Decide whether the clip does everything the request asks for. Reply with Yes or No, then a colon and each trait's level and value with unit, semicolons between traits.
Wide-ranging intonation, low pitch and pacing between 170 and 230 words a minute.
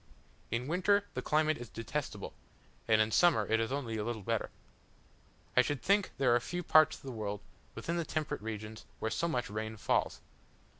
Yes: wide, 6.1 semitones; low, 120 Hz; average, 190 wpm